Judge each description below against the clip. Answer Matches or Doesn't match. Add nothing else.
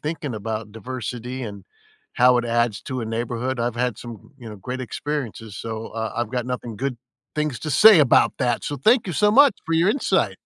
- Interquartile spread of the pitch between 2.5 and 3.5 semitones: Doesn't match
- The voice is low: Matches